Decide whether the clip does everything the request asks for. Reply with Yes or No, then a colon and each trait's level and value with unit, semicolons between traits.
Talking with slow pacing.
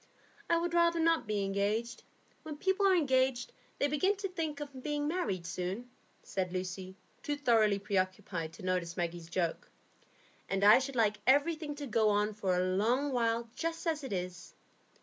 No: average, 170 wpm